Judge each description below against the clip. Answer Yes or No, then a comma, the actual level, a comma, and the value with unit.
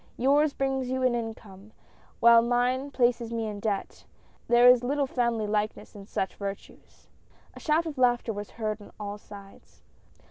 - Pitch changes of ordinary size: Yes, average, 3.4 semitones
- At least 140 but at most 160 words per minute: No, average, 180 wpm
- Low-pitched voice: No, high, 235 Hz